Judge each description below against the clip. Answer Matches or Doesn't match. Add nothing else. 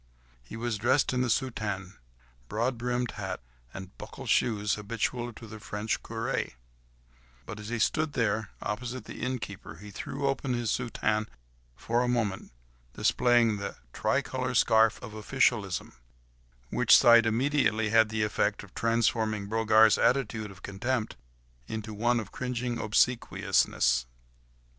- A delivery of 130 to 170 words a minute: Matches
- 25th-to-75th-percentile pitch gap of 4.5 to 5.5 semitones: Doesn't match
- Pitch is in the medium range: Doesn't match